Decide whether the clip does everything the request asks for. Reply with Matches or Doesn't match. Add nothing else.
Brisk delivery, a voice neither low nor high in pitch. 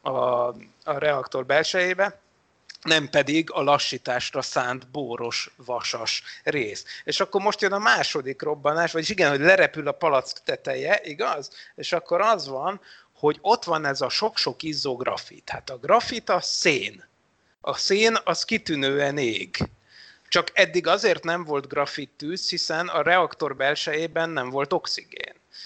Doesn't match